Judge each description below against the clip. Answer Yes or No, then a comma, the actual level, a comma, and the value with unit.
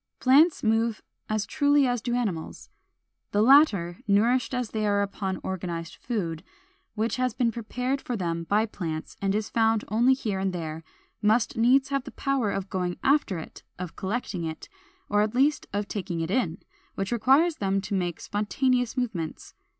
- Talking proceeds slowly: No, average, 175 wpm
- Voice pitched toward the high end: Yes, high, 215 Hz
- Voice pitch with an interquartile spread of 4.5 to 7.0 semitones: Yes, average, 4.8 semitones